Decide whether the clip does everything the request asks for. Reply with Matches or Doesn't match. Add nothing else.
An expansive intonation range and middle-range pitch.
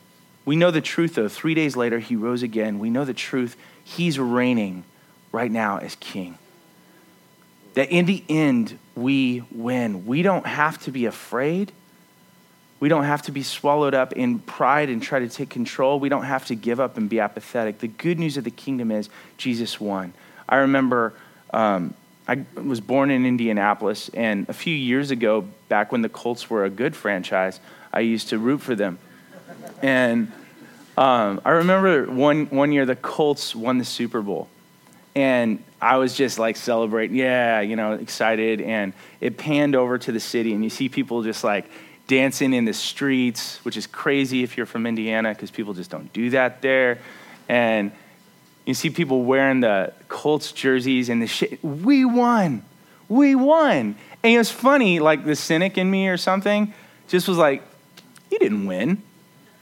Doesn't match